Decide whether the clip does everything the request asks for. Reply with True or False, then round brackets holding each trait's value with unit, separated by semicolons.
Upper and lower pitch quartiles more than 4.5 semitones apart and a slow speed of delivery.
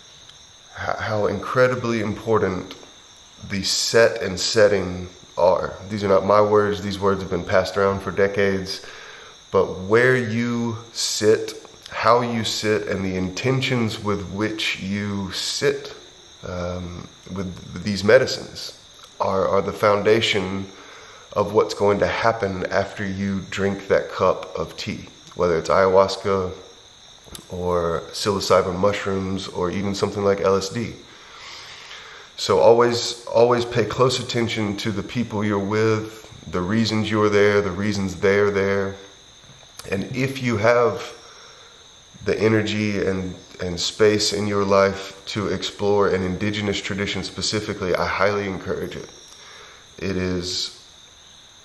False (2.4 semitones; 125 wpm)